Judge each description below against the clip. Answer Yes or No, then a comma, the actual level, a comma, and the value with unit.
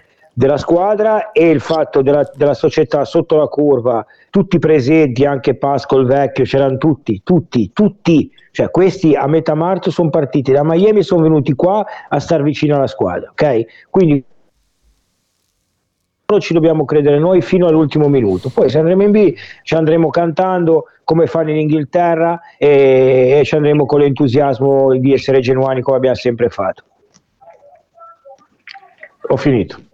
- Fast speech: No, average, 150 wpm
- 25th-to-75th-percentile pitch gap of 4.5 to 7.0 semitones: No, average, 4.1 semitones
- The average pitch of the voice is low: No, medium, 155 Hz